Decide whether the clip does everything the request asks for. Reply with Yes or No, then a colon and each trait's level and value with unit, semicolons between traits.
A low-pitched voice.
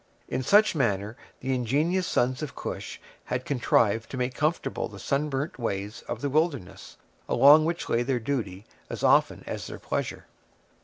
Yes: low, 130 Hz